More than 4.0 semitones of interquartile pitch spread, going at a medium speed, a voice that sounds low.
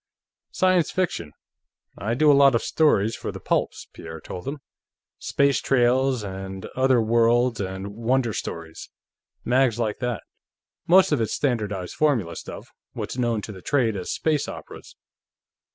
Yes: average, 5.2 semitones; average, 150 wpm; low, 120 Hz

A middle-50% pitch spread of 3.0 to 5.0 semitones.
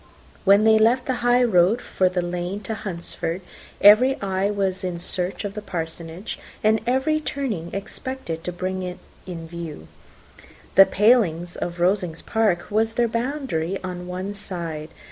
Yes: average, 4.1 semitones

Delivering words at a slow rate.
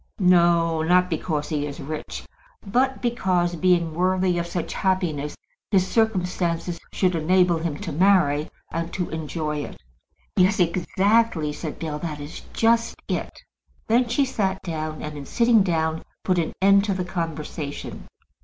No: average, 150 wpm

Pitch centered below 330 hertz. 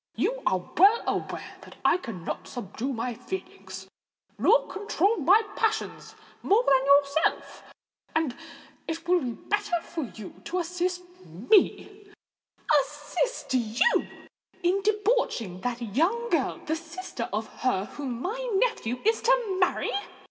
No: very high, 335 Hz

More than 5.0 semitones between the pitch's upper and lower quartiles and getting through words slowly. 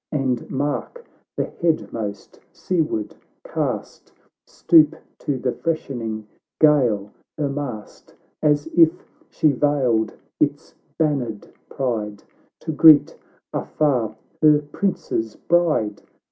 Yes: wide, 5.5 semitones; slow, 100 wpm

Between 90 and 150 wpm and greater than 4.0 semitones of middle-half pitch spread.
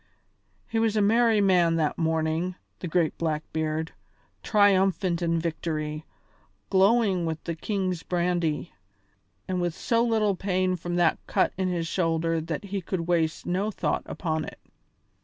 No: average, 145 wpm; average, 3.0 semitones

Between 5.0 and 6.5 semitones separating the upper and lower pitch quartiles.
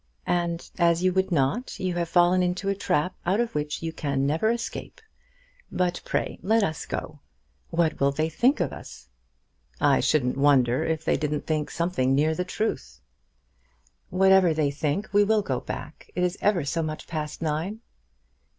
No: average, 3.7 semitones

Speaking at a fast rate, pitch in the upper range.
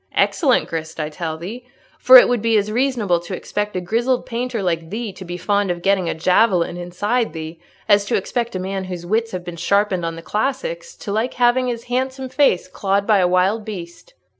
Yes: fast, 215 wpm; high, 200 Hz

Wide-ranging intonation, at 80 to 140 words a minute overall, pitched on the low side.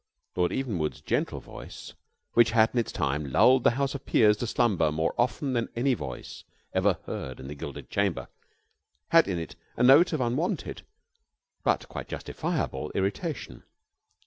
No: wide, 8.6 semitones; average, 160 wpm; low, 115 Hz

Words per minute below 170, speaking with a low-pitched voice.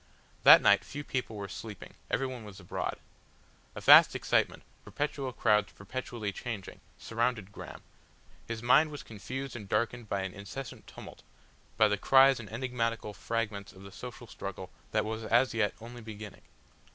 Yes: average, 155 wpm; low, 115 Hz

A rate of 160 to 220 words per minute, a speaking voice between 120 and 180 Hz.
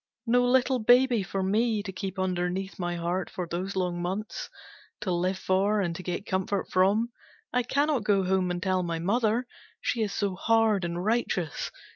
No: average, 180 wpm; high, 195 Hz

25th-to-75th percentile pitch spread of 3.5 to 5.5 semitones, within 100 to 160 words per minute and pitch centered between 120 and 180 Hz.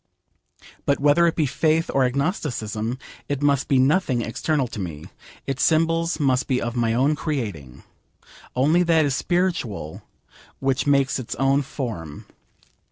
Yes: average, 4.5 semitones; average, 145 wpm; low, 135 Hz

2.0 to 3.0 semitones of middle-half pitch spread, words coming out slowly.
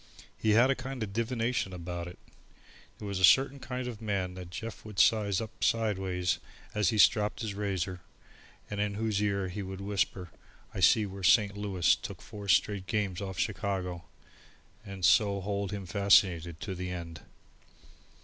No: narrow, 2.5 semitones; average, 175 wpm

